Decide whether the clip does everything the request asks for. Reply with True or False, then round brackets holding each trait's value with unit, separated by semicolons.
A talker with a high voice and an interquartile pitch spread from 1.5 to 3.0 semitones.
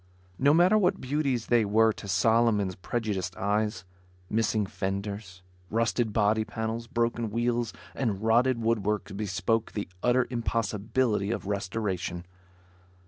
False (110 Hz; 2.7 semitones)